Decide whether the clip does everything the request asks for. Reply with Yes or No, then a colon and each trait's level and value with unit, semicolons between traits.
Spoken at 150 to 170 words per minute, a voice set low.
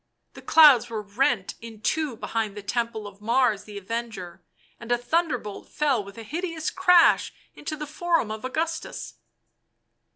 No: average, 160 wpm; high, 235 Hz